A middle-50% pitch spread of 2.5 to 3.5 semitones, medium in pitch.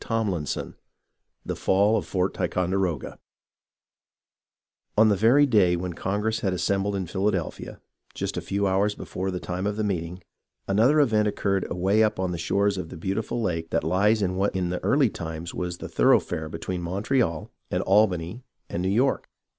No: average, 2.9 semitones; very low, 95 Hz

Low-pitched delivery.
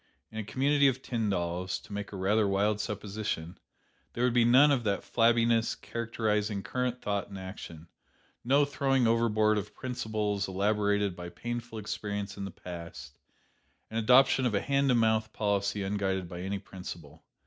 Yes: low, 105 Hz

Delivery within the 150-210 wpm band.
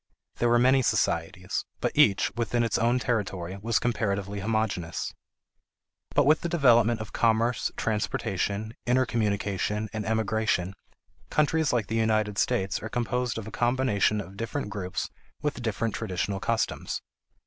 No: slow, 135 wpm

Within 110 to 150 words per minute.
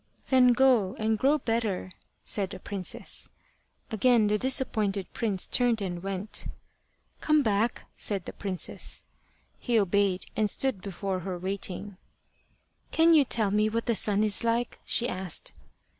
Yes: average, 145 wpm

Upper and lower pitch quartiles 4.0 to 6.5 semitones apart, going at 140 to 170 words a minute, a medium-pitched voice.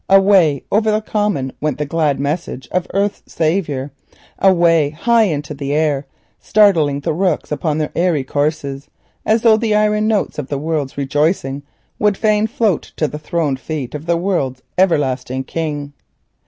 Yes: wide, 5.4 semitones; average, 160 wpm; medium, 155 Hz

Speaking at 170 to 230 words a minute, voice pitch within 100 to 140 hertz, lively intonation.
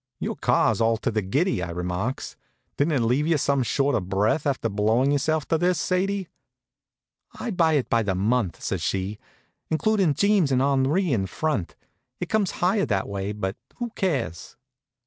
Yes: average, 175 wpm; low, 135 Hz; wide, 8.2 semitones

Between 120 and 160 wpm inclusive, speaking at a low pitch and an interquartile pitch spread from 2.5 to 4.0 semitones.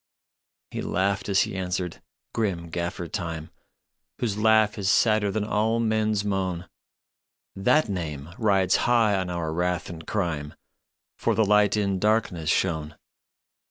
Yes: average, 150 wpm; very low, 95 Hz; average, 3.7 semitones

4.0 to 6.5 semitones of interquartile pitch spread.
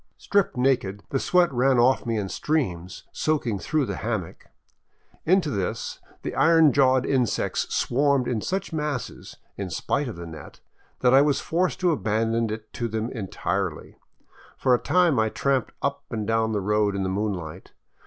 Yes: average, 5.1 semitones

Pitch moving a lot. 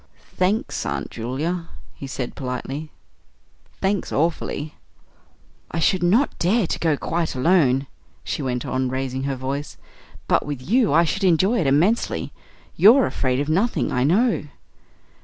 Yes: wide, 5.8 semitones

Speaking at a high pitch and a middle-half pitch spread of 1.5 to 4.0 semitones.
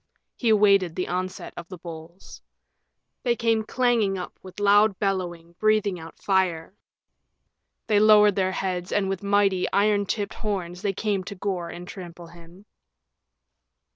Yes: high, 195 Hz; narrow, 2.6 semitones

